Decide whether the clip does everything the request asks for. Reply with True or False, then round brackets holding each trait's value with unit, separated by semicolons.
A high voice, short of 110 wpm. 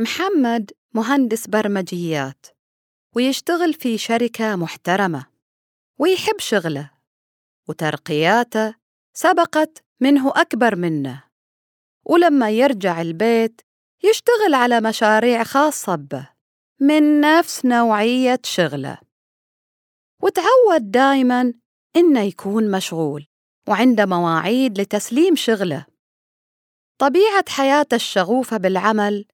True (230 Hz; 80 wpm)